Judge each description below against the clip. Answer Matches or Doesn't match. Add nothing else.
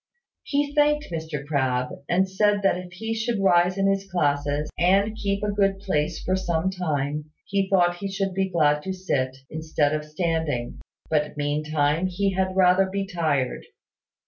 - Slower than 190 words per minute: Matches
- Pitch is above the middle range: Doesn't match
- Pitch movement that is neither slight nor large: Matches